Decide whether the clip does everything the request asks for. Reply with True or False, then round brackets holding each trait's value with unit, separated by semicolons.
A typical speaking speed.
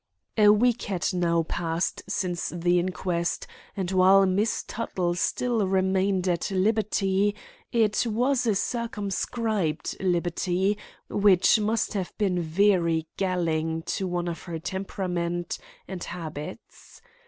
False (120 wpm)